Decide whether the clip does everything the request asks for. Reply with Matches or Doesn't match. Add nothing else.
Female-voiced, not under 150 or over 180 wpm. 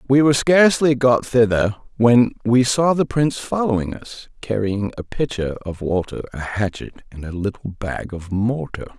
Doesn't match